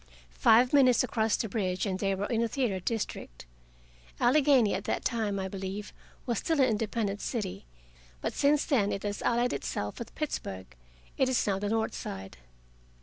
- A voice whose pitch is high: Yes, high, 220 Hz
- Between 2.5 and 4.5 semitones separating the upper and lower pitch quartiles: Yes, average, 3.9 semitones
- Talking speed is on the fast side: No, average, 175 wpm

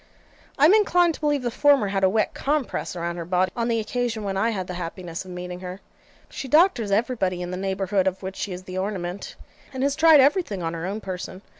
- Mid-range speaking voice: No, high, 195 Hz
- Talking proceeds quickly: Yes, fast, 235 wpm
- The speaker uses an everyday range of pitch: No, wide, 5.9 semitones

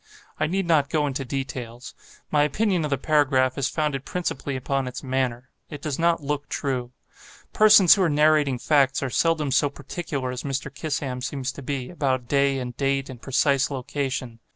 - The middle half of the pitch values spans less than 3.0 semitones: Yes, narrow, 2.5 semitones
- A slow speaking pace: No, average, 180 wpm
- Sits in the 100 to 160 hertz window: Yes, medium, 140 Hz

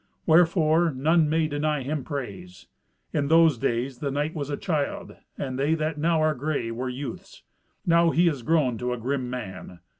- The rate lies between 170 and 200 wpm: Yes, average, 180 wpm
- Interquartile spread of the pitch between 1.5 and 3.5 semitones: No, average, 4.0 semitones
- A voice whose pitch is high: No, medium, 145 Hz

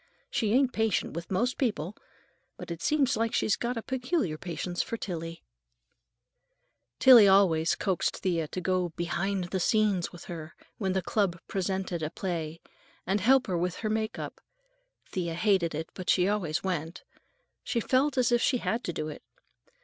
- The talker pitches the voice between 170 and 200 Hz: Yes, high, 190 Hz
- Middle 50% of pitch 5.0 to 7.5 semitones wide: No, average, 4.6 semitones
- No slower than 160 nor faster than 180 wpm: Yes, average, 170 wpm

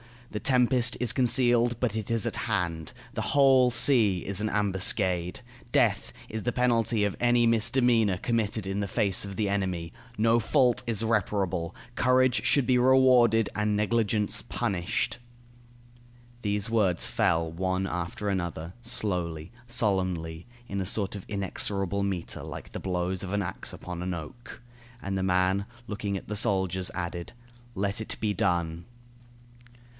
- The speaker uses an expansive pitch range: No, average, 3.9 semitones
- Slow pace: No, average, 150 wpm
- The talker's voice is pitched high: No, low, 100 Hz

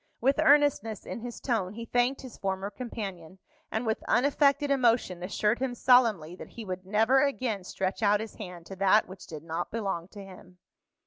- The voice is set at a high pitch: Yes, high, 215 Hz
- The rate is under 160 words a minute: No, average, 185 wpm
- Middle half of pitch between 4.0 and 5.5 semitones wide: Yes, average, 4.6 semitones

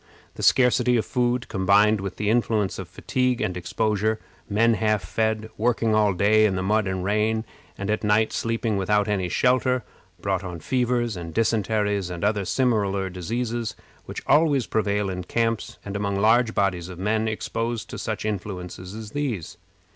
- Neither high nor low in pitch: No, low, 105 Hz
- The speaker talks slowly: No, average, 170 wpm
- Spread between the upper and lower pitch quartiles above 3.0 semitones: No, average, 2.7 semitones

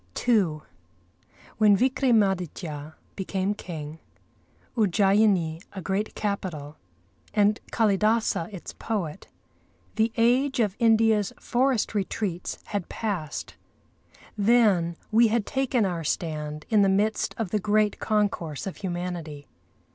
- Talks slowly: Yes, slow, 110 wpm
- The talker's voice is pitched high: Yes, high, 200 Hz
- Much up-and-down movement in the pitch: No, average, 4.2 semitones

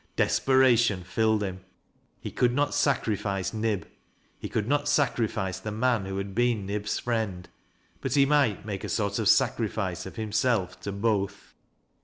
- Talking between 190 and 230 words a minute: No, average, 160 wpm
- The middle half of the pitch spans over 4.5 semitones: No, average, 3.7 semitones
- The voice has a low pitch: Yes, low, 110 Hz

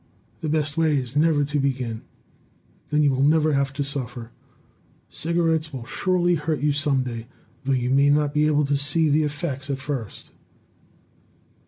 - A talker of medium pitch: Yes, medium, 145 Hz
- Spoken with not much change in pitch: Yes, narrow, 2.1 semitones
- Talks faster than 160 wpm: Yes, average, 170 wpm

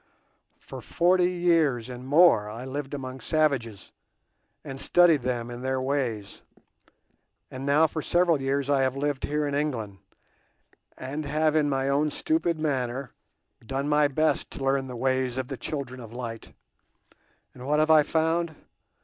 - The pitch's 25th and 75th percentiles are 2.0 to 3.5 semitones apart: Yes, average, 3.1 semitones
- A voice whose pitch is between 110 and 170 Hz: Yes, medium, 140 Hz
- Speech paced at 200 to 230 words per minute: No, average, 160 wpm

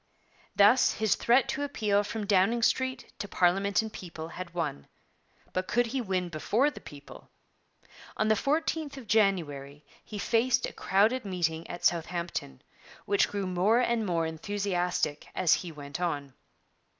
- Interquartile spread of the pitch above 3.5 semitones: Yes, average, 4.9 semitones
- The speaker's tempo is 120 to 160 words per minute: Yes, average, 150 wpm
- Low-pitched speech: No, high, 195 Hz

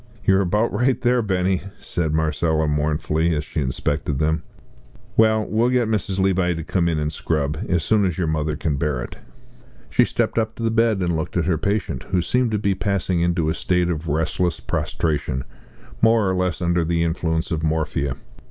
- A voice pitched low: Yes, very low, 85 Hz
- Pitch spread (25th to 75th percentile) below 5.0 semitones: Yes, average, 4.1 semitones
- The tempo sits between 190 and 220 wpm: Yes, average, 195 wpm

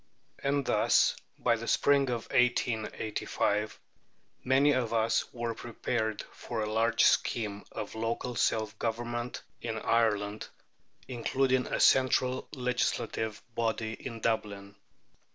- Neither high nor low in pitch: No, low, 115 Hz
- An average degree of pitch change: No, narrow, 2.2 semitones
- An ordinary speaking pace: No, slow, 115 wpm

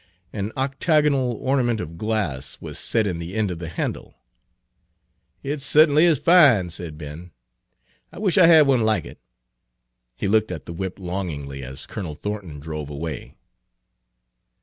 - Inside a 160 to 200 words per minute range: No, average, 150 wpm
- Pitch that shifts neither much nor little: No, wide, 8.6 semitones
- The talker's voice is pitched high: No, low, 100 Hz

